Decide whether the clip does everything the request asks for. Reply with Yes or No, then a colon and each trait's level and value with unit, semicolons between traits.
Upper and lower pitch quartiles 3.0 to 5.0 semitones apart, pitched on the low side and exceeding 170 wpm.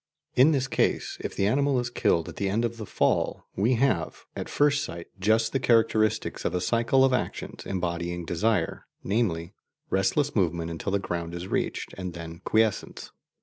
No: wide, 5.5 semitones; low, 105 Hz; average, 180 wpm